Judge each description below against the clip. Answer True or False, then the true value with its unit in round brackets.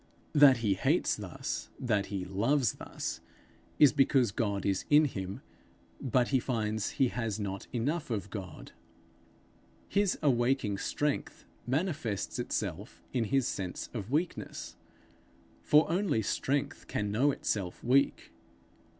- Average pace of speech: False (125 wpm)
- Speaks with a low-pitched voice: True (120 Hz)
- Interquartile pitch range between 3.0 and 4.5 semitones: False (5.6 semitones)